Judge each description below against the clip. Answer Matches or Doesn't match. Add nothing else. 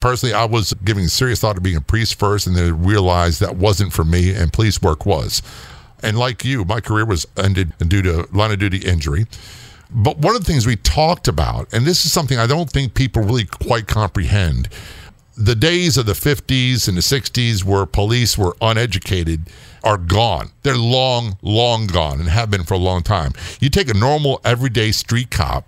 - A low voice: Matches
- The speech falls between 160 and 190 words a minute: Doesn't match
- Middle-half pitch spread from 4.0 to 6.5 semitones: Matches